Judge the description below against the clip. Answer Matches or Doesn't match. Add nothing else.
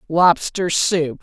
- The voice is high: Doesn't match